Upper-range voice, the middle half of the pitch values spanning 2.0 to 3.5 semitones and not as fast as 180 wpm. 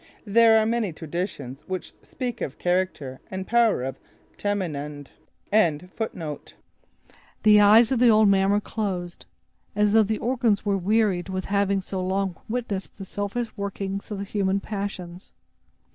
Yes: high, 200 Hz; average, 3.0 semitones; average, 145 wpm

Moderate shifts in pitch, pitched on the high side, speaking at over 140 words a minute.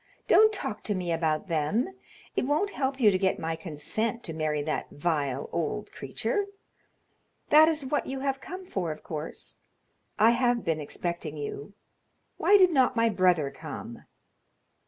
No: wide, 8.8 semitones; high, 200 Hz; average, 160 wpm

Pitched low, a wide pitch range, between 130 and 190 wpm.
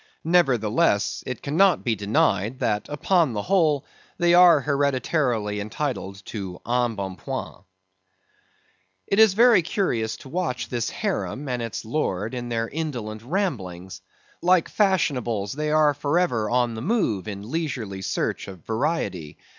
Yes: low, 125 Hz; wide, 7.2 semitones; average, 140 wpm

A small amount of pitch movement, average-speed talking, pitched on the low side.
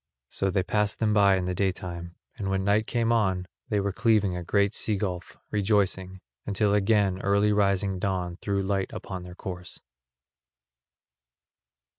Yes: narrow, 1.8 semitones; average, 160 wpm; low, 100 Hz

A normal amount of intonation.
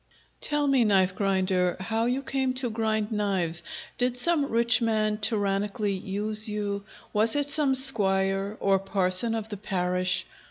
Yes: average, 3.5 semitones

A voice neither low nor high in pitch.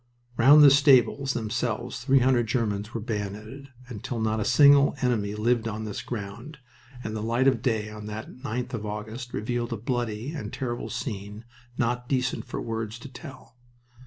No: low, 120 Hz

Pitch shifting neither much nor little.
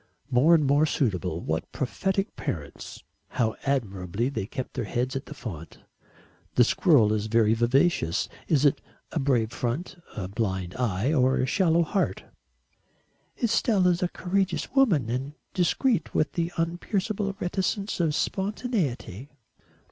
No: wide, 7.9 semitones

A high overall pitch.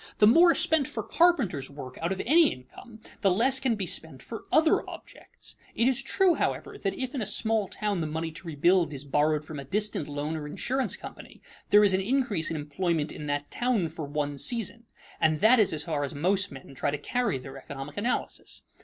No: medium, 180 Hz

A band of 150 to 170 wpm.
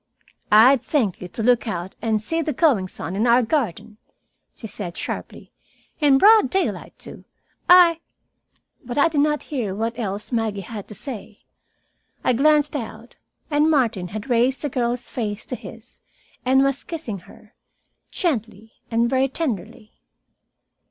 Yes: average, 155 wpm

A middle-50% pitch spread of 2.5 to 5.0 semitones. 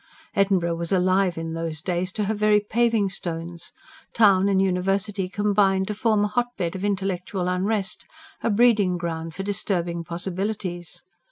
Yes: average, 2.8 semitones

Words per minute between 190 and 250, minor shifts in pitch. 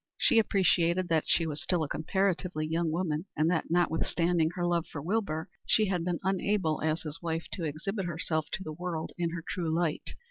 Yes: average, 200 wpm; narrow, 2.3 semitones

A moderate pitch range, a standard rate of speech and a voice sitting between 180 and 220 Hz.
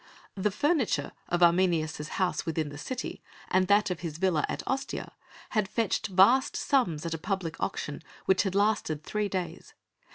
Yes: average, 4.3 semitones; average, 165 wpm; medium, 185 Hz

